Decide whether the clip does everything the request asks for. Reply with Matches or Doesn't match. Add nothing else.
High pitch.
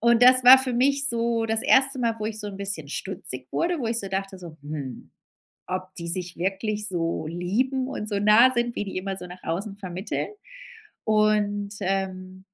Matches